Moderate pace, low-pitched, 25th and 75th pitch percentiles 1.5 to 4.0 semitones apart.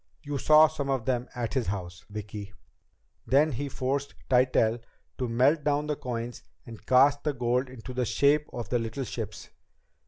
Yes: average, 175 wpm; low, 130 Hz; average, 3.4 semitones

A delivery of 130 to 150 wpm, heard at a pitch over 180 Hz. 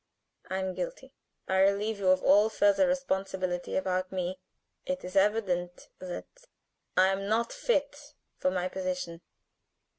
Yes: average, 140 wpm; high, 190 Hz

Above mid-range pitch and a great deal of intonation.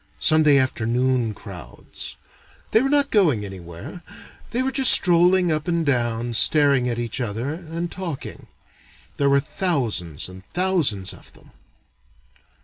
No: medium, 140 Hz; wide, 7.2 semitones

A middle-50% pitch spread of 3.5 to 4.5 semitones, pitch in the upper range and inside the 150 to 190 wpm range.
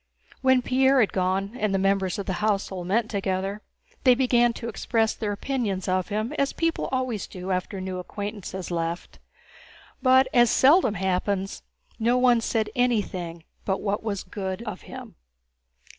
Yes: average, 4.2 semitones; high, 205 Hz; average, 165 wpm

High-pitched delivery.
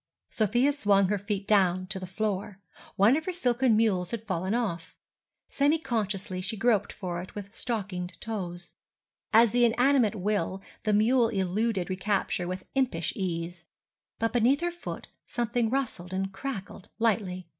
Yes: high, 210 Hz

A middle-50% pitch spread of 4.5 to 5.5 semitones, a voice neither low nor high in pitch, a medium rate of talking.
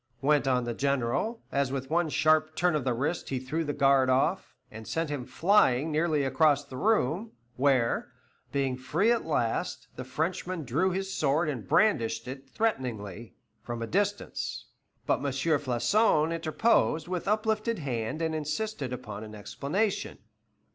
Yes: average, 5.2 semitones; medium, 145 Hz; average, 155 wpm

